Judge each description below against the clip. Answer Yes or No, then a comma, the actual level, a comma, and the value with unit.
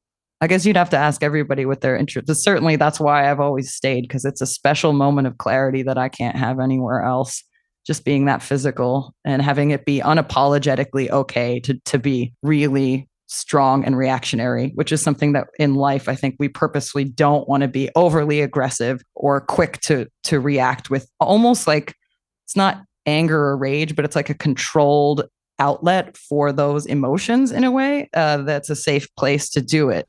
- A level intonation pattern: Yes, narrow, 2.2 semitones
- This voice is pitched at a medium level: Yes, medium, 145 Hz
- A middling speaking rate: Yes, average, 190 wpm